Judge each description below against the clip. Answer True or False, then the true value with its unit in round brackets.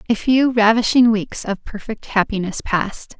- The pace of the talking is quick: False (150 wpm)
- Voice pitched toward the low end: False (220 Hz)